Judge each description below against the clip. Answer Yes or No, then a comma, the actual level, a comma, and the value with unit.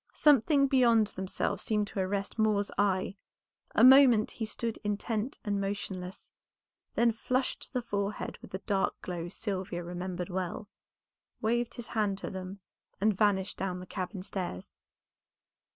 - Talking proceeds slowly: No, average, 145 wpm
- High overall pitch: Yes, high, 205 Hz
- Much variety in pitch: No, average, 3.2 semitones